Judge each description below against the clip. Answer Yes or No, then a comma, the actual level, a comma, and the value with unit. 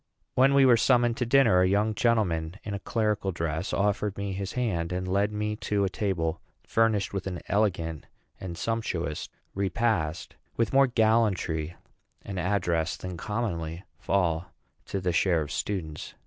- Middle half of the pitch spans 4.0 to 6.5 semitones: Yes, average, 4.3 semitones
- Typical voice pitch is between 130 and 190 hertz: No, low, 100 Hz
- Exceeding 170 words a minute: No, average, 160 wpm